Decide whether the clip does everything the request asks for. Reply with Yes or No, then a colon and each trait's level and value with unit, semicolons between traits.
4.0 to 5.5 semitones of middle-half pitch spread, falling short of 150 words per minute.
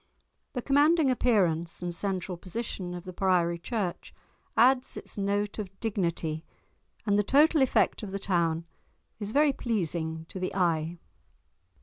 Yes: average, 5.1 semitones; average, 140 wpm